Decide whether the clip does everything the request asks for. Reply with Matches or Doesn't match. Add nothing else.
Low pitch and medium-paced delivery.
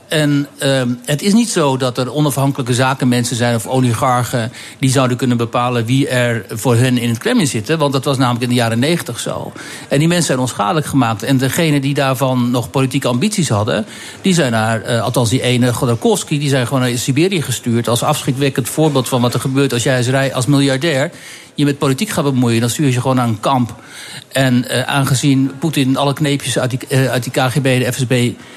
Doesn't match